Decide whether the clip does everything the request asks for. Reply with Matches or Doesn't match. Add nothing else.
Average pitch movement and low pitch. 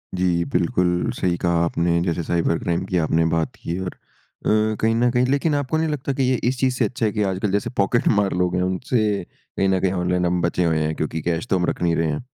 Matches